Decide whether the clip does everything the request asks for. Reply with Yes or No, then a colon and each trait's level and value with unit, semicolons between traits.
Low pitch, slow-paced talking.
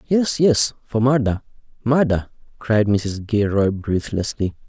Yes: low, 115 Hz; slow, 105 wpm